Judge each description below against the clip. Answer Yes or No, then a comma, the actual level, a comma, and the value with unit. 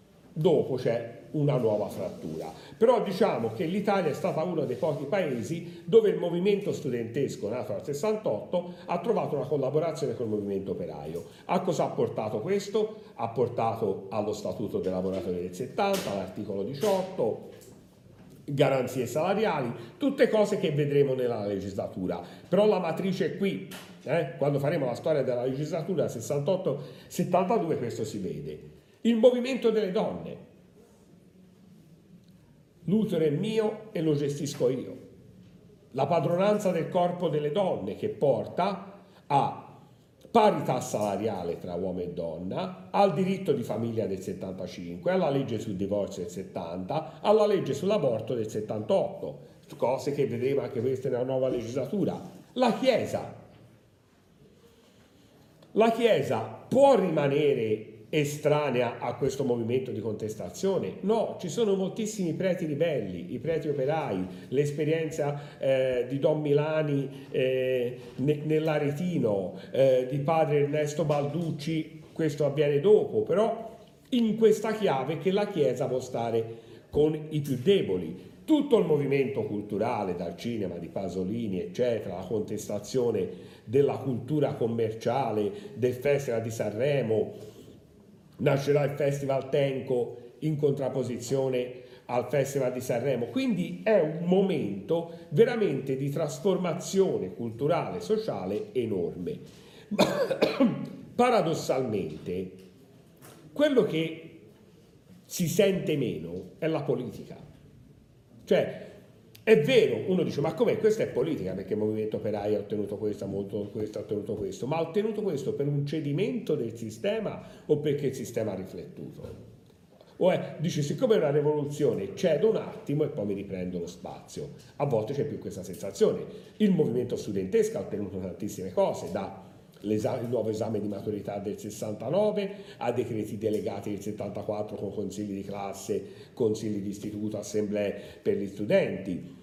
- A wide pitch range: Yes, wide, 8.4 semitones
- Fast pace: No, average, 135 wpm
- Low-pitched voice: No, medium, 145 Hz